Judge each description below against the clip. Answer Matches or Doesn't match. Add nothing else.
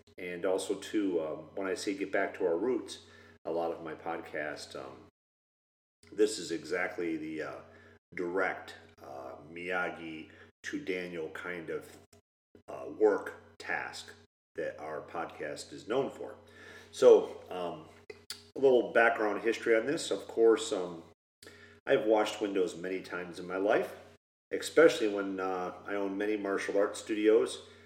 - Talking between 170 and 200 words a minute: Doesn't match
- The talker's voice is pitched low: Matches